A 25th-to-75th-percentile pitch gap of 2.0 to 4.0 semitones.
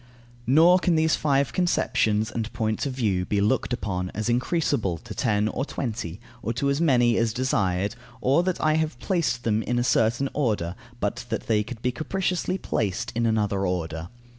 No: average, 4.9 semitones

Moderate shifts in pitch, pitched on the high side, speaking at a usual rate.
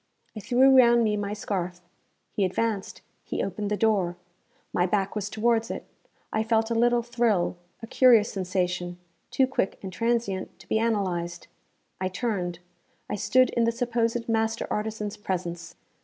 Yes: average, 3.7 semitones; high, 215 Hz; average, 155 wpm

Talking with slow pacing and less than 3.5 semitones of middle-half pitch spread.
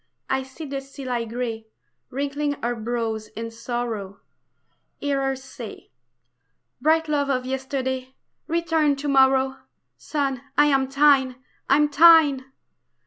Yes: slow, 125 wpm; narrow, 2.6 semitones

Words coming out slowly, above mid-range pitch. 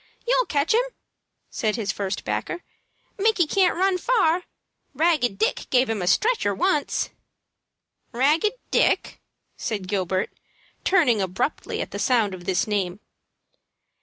Yes: slow, 130 wpm; very high, 250 Hz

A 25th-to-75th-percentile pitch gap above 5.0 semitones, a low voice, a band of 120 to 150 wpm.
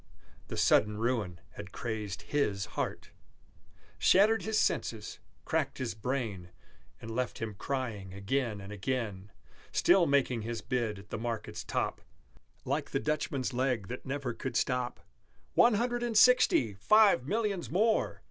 Yes: wide, 5.4 semitones; low, 125 Hz; average, 140 wpm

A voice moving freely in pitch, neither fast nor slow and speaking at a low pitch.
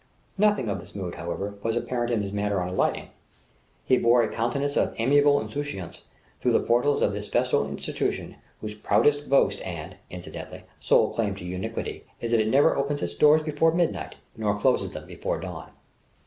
Yes: wide, 5.9 semitones; average, 180 wpm; low, 115 Hz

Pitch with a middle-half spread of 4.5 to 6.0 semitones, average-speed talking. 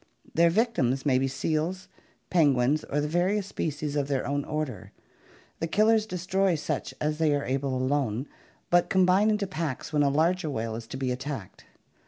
Yes: average, 5.1 semitones; average, 175 wpm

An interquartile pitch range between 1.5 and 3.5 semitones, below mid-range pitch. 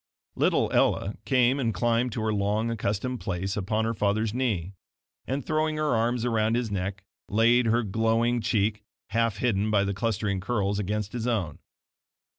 Yes: average, 2.8 semitones; low, 110 Hz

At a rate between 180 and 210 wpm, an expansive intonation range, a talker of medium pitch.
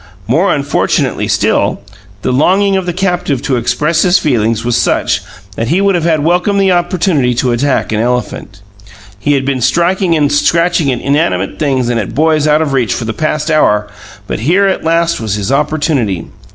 Yes: average, 185 wpm; wide, 5.8 semitones; medium, 145 Hz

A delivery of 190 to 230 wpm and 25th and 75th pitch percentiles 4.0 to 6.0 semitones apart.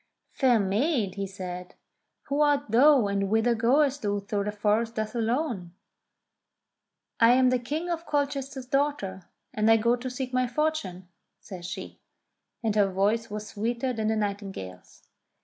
No: average, 160 wpm; average, 4.6 semitones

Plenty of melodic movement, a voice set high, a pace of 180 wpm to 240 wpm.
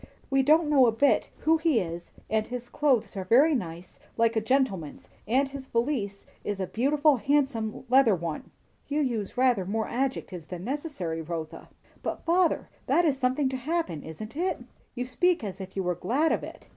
Yes: wide, 6.7 semitones; high, 245 Hz; average, 185 wpm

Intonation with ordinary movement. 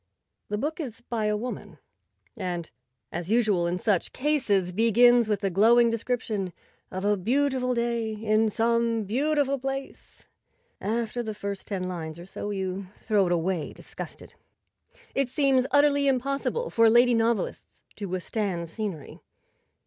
Yes: average, 4.1 semitones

